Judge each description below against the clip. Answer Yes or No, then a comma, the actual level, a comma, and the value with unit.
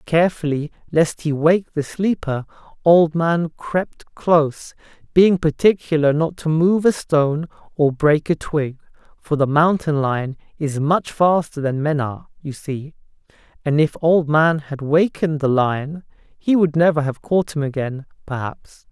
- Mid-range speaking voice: Yes, medium, 155 Hz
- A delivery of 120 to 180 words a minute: Yes, average, 155 wpm